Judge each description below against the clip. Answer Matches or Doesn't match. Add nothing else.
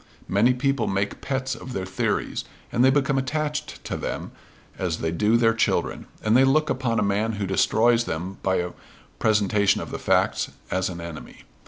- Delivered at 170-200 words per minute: Matches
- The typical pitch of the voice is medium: Doesn't match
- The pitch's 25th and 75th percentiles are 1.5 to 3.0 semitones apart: Doesn't match